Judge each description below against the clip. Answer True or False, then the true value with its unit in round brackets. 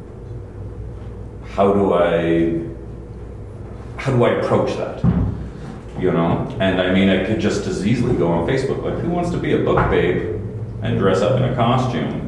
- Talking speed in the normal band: True (170 wpm)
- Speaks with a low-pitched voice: True (105 Hz)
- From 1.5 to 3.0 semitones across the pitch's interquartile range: False (3.6 semitones)